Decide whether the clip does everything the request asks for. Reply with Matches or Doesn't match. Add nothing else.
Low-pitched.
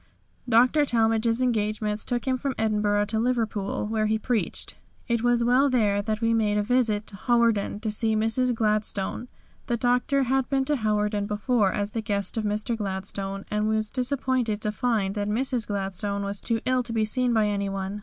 Doesn't match